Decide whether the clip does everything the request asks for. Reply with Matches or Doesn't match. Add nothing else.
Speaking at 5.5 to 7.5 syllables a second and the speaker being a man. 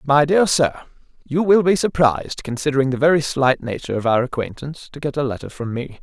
Matches